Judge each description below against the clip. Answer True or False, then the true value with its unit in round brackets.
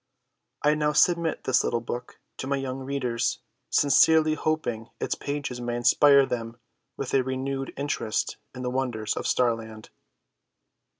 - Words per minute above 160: False (140 wpm)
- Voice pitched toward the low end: True (130 Hz)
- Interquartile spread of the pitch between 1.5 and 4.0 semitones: True (3.0 semitones)